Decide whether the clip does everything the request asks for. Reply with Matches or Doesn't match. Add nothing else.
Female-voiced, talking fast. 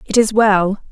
Doesn't match